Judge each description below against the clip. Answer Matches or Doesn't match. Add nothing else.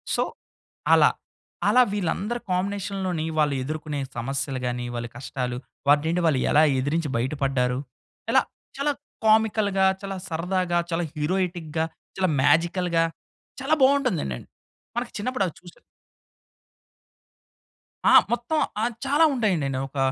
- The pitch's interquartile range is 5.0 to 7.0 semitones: Matches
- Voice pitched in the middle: Matches